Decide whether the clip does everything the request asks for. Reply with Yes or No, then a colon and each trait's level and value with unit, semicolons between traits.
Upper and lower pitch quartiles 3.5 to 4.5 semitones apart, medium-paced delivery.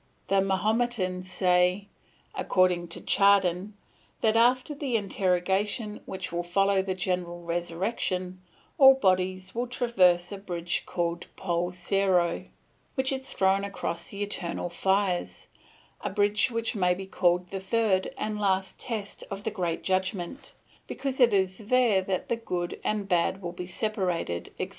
No: average, 2.8 semitones; average, 145 wpm